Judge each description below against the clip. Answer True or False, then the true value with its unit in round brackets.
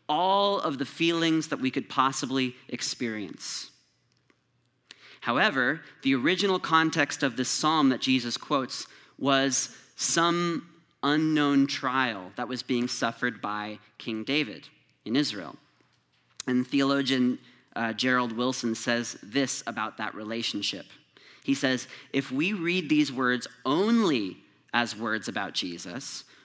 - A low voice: True (130 Hz)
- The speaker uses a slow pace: True (125 wpm)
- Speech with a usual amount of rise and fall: True (3.9 semitones)